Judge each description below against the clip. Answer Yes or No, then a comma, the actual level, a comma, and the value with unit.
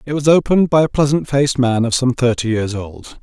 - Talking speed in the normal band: No, fast, 240 wpm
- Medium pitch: No, low, 130 Hz